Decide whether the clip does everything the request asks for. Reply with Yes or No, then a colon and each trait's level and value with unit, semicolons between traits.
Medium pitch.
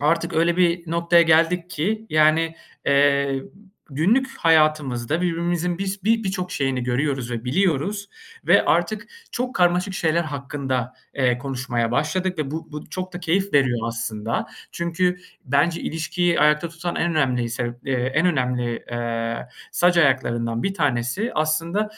Yes: medium, 155 Hz